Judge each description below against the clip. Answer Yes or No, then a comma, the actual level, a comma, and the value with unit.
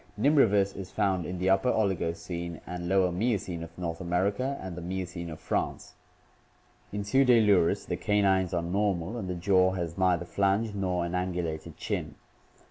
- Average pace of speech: Yes, average, 160 wpm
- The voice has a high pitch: No, very low, 95 Hz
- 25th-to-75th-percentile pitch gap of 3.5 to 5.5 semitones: No, narrow, 2.5 semitones